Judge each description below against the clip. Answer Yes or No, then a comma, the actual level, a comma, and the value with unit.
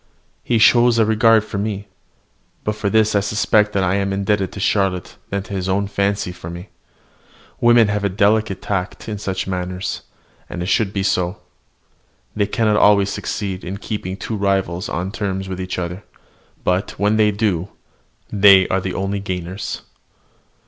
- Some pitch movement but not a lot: No, narrow, 2.0 semitones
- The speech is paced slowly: No, average, 170 wpm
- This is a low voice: Yes, low, 100 Hz